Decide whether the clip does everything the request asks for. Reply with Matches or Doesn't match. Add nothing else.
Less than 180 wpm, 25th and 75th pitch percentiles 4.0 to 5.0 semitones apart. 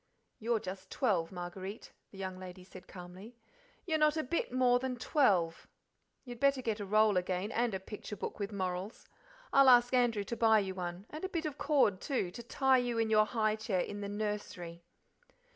Doesn't match